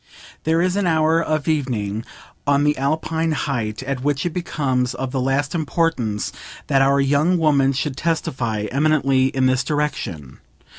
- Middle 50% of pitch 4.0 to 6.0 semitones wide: No, average, 3.3 semitones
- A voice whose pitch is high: No, medium, 140 Hz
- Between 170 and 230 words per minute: No, average, 155 wpm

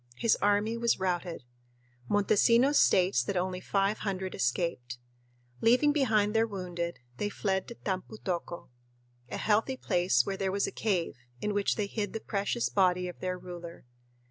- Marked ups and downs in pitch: No, average, 3.2 semitones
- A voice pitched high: Yes, high, 195 Hz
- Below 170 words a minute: Yes, average, 160 wpm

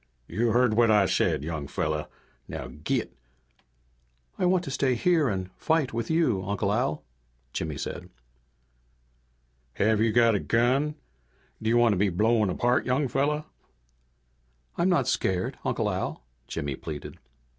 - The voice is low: Yes, low, 115 Hz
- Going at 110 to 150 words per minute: Yes, average, 145 wpm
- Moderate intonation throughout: No, wide, 6.1 semitones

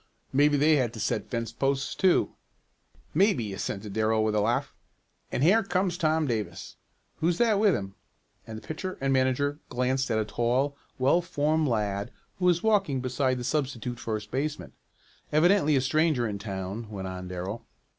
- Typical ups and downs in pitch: No, wide, 6.0 semitones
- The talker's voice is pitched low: Yes, low, 130 Hz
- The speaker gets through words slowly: No, average, 170 wpm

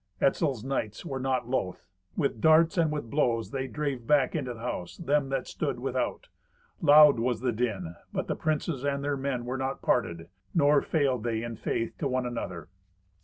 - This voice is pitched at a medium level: No, low, 130 Hz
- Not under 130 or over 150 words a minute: No, average, 185 wpm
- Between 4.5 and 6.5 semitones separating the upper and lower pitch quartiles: No, average, 3.6 semitones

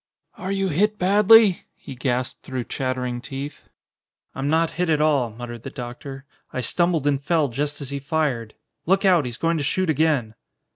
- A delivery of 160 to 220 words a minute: Yes, average, 180 wpm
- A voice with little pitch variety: No, average, 4.7 semitones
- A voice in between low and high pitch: Yes, medium, 145 Hz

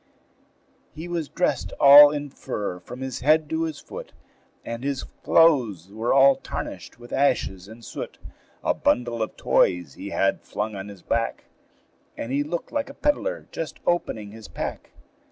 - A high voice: No, low, 130 Hz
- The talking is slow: No, average, 165 wpm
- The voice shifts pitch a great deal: Yes, wide, 6.0 semitones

